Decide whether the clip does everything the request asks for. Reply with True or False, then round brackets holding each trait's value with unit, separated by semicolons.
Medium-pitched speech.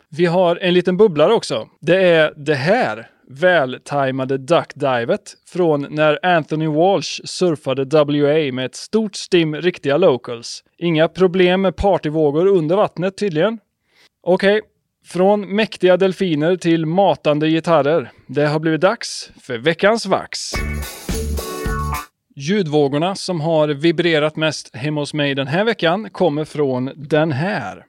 True (160 Hz)